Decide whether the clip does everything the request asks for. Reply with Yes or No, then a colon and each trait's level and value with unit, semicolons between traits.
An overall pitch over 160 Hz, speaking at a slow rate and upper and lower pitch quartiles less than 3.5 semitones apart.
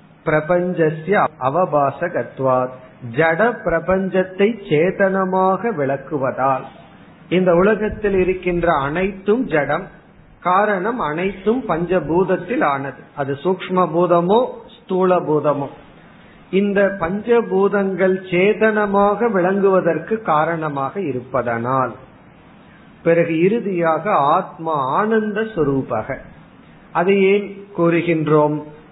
No: medium, 180 Hz; slow, 70 wpm; average, 4.3 semitones